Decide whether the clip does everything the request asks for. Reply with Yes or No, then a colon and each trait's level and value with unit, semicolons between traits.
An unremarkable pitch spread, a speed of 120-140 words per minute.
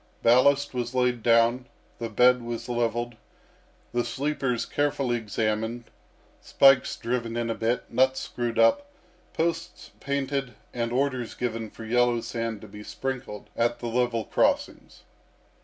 No: narrow, 2.1 semitones; slow, 135 wpm